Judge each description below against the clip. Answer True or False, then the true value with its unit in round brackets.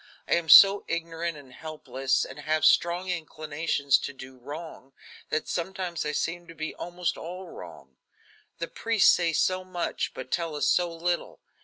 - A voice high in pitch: False (165 Hz)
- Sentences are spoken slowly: False (170 wpm)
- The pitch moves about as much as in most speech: True (3.0 semitones)